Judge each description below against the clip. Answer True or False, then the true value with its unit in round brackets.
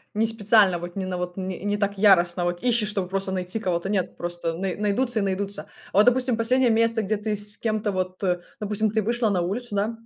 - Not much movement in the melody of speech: False (3.0 semitones)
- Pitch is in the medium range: False (205 Hz)